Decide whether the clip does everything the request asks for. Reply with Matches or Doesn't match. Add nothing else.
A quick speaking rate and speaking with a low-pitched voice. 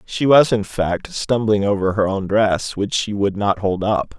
Matches